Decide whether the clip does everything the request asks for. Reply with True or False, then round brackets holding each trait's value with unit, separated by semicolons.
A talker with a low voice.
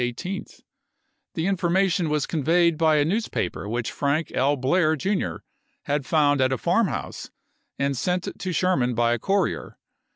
False (155 Hz)